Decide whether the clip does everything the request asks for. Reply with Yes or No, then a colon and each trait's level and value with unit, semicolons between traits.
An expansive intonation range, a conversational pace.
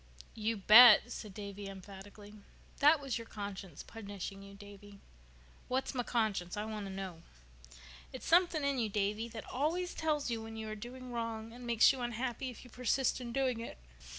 No: average, 3.7 semitones; average, 180 wpm